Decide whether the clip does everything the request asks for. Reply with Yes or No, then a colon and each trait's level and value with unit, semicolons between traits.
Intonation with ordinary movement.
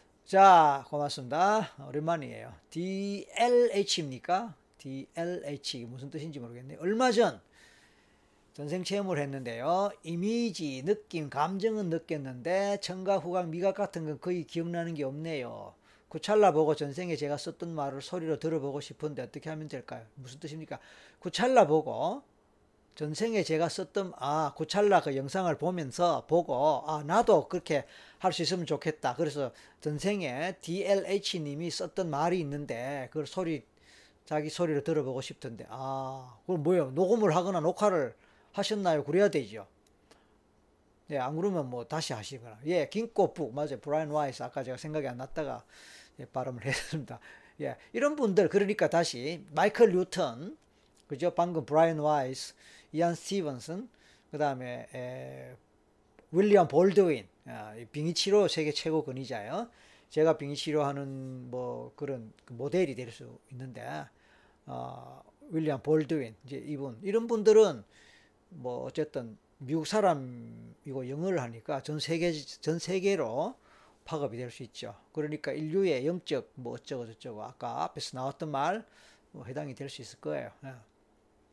Yes: average, 4.7 semitones